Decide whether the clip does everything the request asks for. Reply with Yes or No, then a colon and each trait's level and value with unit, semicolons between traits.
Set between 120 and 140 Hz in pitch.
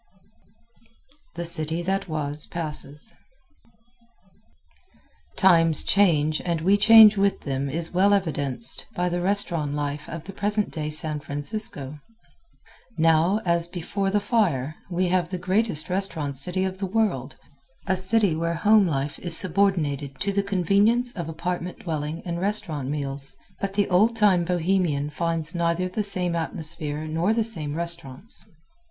No: medium, 170 Hz